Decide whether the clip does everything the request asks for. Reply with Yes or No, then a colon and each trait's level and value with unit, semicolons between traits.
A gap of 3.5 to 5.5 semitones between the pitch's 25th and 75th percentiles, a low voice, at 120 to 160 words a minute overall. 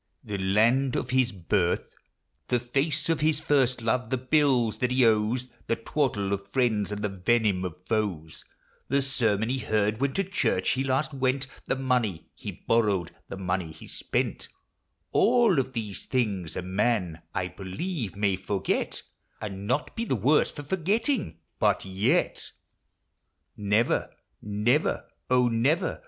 Yes: average, 5.1 semitones; low, 115 Hz; average, 150 wpm